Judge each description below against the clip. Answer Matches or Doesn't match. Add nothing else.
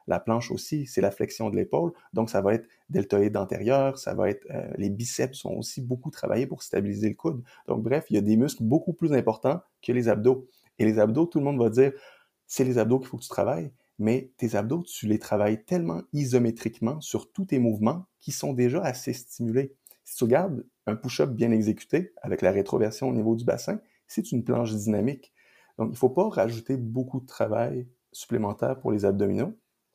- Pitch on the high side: Doesn't match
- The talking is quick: Doesn't match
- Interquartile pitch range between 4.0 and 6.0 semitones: Doesn't match